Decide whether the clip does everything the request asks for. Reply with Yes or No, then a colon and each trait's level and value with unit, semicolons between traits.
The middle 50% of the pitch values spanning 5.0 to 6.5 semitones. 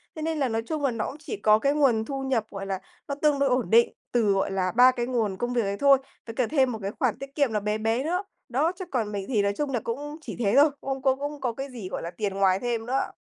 No: average, 4.6 semitones